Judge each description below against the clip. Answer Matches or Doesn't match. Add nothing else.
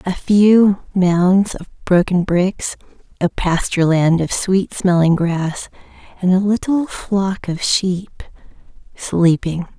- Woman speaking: Matches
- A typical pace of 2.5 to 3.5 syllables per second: Matches